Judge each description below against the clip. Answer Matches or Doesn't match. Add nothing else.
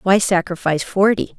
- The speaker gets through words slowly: Matches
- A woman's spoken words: Matches